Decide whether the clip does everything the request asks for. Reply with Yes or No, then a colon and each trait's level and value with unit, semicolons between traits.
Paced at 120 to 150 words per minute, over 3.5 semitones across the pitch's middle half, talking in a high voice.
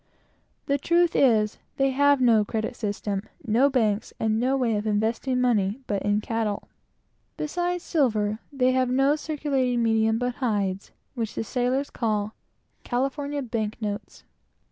Yes: average, 145 wpm; average, 4.1 semitones; high, 240 Hz